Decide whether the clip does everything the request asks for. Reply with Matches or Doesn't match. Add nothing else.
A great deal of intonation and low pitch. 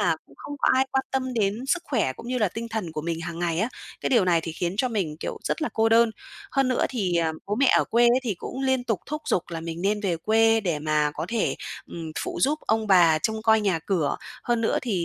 Doesn't match